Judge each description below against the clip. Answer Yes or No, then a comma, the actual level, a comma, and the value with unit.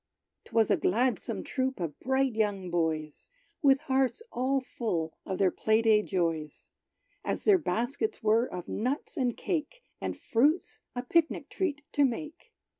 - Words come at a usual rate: Yes, average, 155 wpm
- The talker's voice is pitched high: Yes, high, 245 Hz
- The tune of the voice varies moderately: No, wide, 5.9 semitones